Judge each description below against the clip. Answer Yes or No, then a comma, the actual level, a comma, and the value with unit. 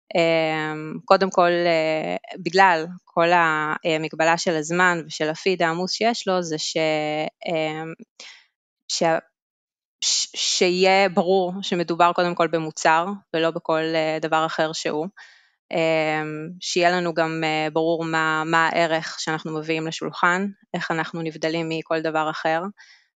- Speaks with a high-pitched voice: No, medium, 165 Hz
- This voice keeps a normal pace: Yes, average, 120 wpm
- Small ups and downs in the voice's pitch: Yes, narrow, 2.0 semitones